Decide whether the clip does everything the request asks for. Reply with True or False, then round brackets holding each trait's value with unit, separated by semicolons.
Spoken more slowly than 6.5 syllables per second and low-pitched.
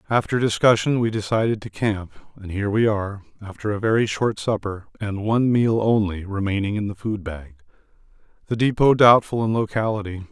True (5.6 syllables/s; 105 Hz)